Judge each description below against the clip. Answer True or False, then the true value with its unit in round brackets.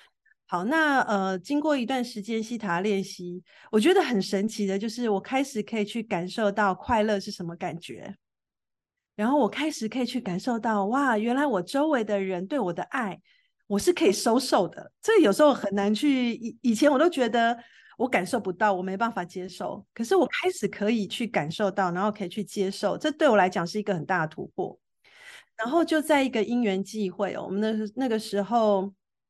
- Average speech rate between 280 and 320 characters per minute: True (285 characters per minute)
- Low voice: False (215 Hz)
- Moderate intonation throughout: True (4.6 semitones)